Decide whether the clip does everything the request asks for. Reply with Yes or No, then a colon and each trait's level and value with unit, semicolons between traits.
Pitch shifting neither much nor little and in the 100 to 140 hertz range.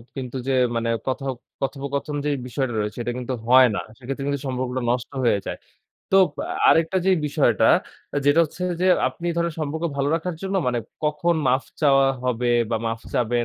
Yes: average, 3.2 semitones; low, 135 Hz